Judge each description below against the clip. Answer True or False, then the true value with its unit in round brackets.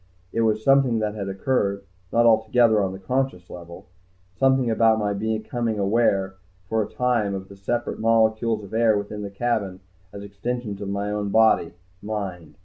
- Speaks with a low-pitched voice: True (110 Hz)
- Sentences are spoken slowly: False (170 wpm)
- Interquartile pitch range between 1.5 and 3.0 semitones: True (2.6 semitones)